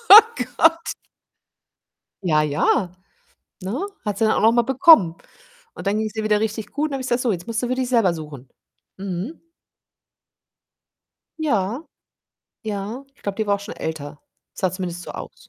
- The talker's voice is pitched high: Yes, high, 215 Hz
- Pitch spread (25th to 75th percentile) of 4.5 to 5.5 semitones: Yes, average, 5.1 semitones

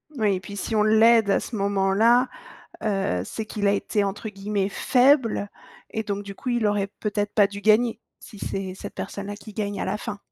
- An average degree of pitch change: No, narrow, 1.7 semitones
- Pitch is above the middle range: Yes, high, 205 Hz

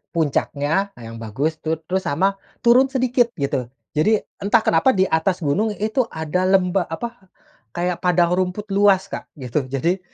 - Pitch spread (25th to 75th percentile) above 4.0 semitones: Yes, average, 4.6 semitones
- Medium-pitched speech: Yes, medium, 180 Hz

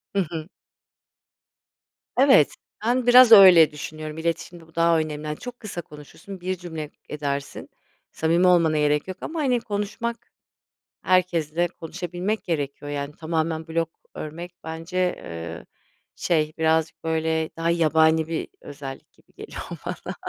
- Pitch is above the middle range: No, medium, 165 Hz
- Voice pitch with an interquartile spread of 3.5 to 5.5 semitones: No, average, 2.8 semitones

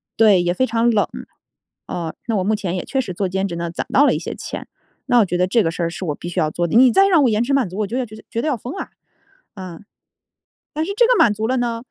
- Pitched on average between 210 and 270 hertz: Yes, high, 215 Hz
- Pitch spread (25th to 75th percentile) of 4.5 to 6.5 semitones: Yes, wide, 5.4 semitones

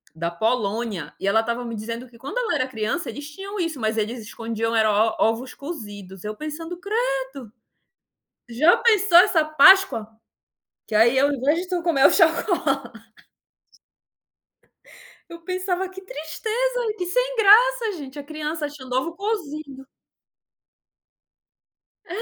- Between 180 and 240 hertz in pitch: No, very high, 290 Hz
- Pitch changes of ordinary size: No, wide, 7.9 semitones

